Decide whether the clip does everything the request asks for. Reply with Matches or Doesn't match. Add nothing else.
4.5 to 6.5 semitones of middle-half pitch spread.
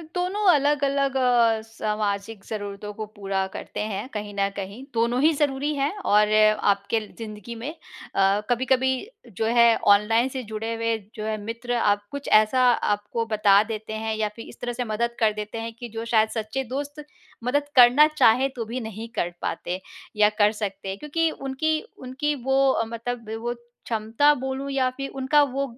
Doesn't match